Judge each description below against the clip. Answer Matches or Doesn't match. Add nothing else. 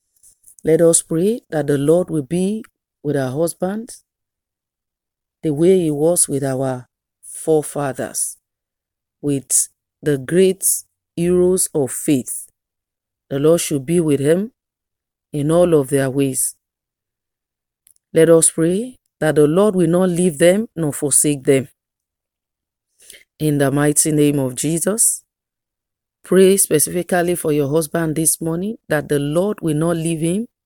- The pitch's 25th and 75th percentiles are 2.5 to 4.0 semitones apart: Matches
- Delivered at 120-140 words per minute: Matches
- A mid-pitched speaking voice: Matches